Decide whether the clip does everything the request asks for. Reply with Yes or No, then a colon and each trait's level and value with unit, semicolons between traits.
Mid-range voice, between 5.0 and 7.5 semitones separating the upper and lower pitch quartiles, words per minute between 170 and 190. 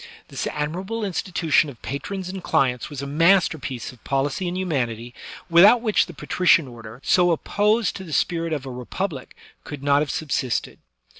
Yes: medium, 155 Hz; wide, 5.4 semitones; average, 180 wpm